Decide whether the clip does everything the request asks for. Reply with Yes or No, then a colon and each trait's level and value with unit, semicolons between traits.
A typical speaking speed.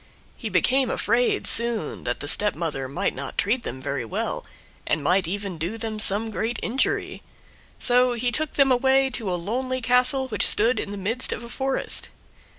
Yes: average, 180 wpm